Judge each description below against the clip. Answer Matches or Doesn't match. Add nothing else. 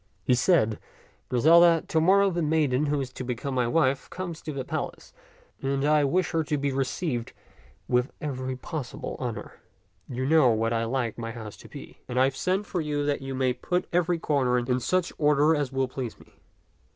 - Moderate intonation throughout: Matches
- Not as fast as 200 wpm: Doesn't match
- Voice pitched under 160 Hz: Matches